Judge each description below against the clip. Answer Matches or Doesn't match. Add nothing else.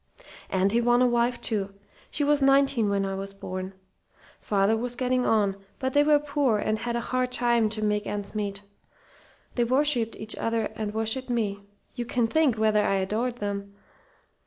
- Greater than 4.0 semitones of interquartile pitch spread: Doesn't match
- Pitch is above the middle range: Matches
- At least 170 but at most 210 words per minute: Matches